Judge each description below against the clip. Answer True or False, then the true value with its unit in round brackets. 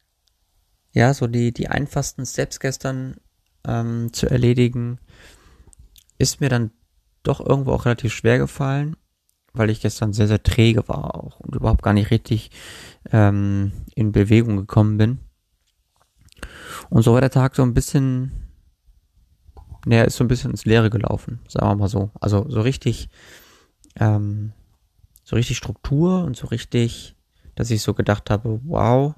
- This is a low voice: True (110 Hz)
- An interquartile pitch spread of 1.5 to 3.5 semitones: False (4.0 semitones)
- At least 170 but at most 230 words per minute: False (150 wpm)